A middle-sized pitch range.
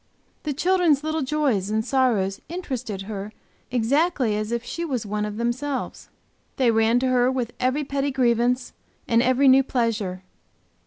Yes: average, 3.9 semitones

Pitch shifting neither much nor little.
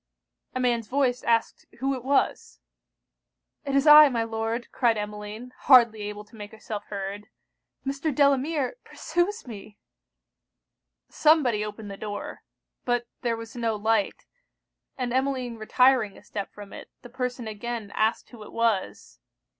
Yes: average, 3.6 semitones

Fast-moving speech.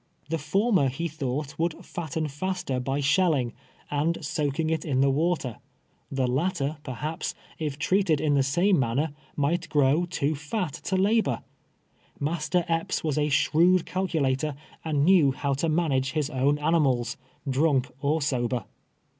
No: average, 155 wpm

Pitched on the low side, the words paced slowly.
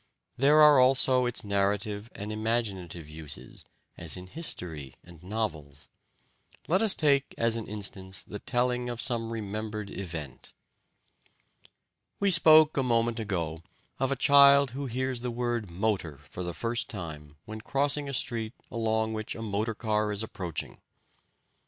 No: low, 110 Hz; average, 145 wpm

